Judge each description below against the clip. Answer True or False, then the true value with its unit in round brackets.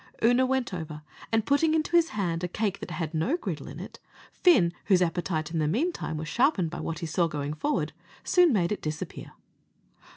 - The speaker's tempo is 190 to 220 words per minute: True (200 wpm)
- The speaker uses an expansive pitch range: True (8.1 semitones)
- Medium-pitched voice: True (180 Hz)